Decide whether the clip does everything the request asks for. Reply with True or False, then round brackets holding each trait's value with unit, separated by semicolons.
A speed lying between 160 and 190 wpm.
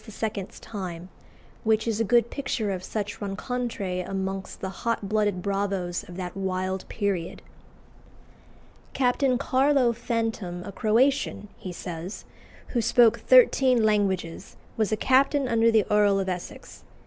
False (135 wpm)